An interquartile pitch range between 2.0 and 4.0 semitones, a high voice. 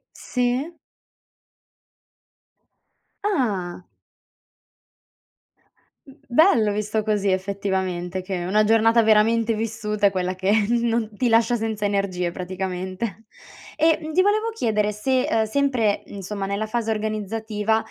Yes: average, 2.7 semitones; high, 215 Hz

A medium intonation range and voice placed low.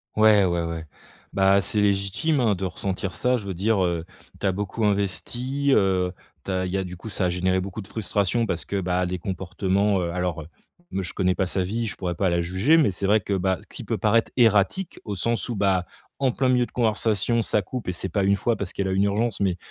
Yes: average, 3.0 semitones; low, 100 Hz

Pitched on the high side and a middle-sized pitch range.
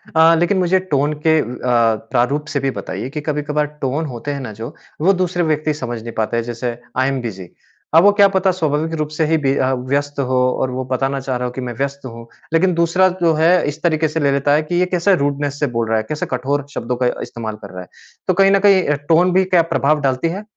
No: medium, 145 Hz; average, 4.5 semitones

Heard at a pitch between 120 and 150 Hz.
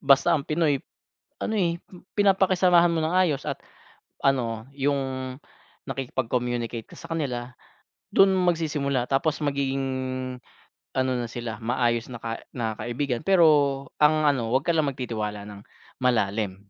Yes: low, 135 Hz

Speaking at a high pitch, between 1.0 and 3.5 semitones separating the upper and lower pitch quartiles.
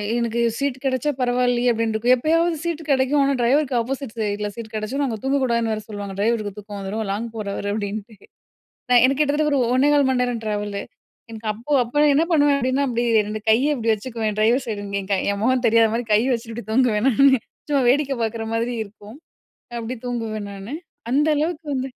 No: high, 235 Hz; average, 3.9 semitones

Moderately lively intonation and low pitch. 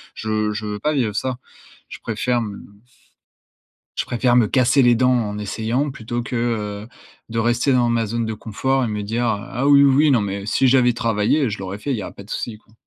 Yes: average, 3.0 semitones; low, 115 Hz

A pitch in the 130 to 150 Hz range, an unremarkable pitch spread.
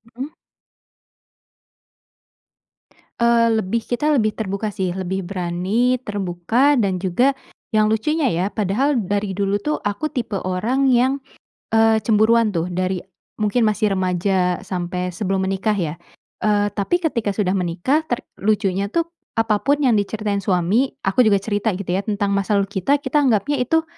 No: high, 205 Hz; average, 3.8 semitones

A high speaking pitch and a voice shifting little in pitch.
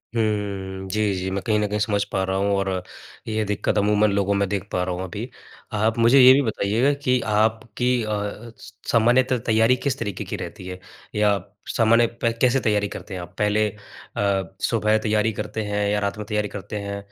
No: low, 105 Hz; narrow, 1.9 semitones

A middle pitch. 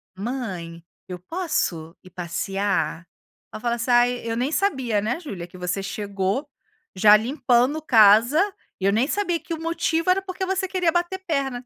No: high, 240 Hz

